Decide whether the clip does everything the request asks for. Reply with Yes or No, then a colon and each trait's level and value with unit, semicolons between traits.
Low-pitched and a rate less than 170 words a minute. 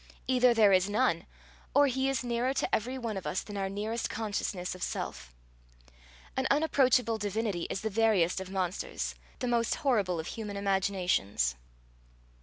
No: high, 210 Hz; average, 160 wpm